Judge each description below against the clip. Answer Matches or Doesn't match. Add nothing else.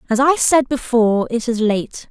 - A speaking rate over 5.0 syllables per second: Doesn't match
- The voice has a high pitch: Matches